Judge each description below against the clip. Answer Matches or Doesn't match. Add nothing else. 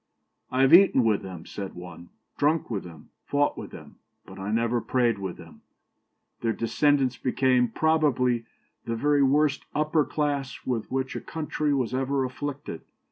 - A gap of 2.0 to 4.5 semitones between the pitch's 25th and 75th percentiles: Matches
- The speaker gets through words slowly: Doesn't match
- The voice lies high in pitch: Doesn't match